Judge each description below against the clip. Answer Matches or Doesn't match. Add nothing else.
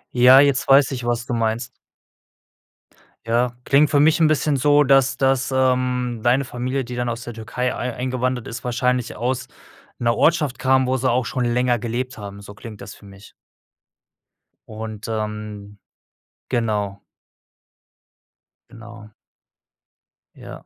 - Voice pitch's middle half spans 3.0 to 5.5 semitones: Doesn't match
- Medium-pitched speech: Doesn't match